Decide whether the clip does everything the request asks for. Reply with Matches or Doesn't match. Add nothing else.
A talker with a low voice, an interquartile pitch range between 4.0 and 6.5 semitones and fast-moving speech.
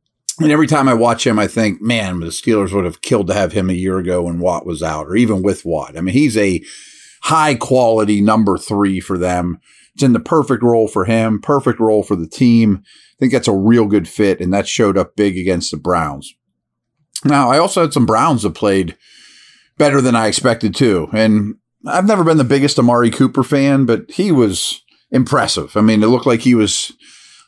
Matches